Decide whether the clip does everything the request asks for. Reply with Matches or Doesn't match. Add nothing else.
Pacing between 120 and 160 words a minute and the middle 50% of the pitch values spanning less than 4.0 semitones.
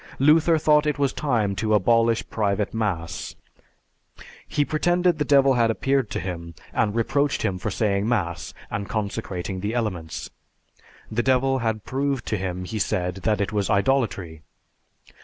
Doesn't match